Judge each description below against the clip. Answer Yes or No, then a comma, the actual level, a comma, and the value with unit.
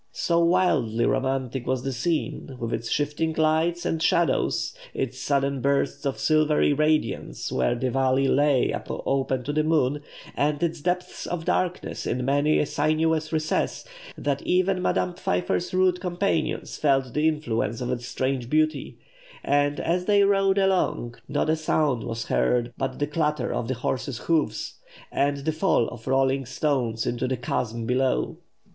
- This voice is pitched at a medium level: Yes, medium, 145 Hz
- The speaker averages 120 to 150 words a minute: No, average, 160 wpm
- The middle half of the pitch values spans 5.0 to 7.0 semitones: No, average, 3.7 semitones